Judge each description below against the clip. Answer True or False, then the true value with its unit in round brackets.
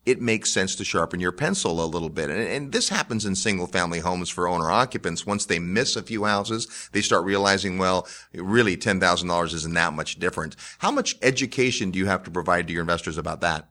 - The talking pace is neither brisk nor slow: False (215 wpm)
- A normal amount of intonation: True (3.3 semitones)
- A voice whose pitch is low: True (95 Hz)